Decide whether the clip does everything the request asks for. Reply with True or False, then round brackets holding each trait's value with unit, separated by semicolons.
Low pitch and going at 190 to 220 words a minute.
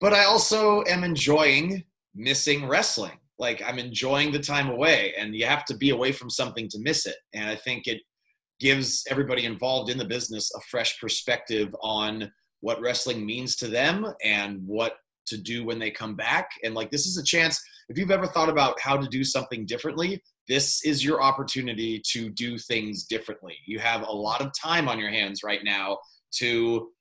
True (125 Hz; 195 wpm)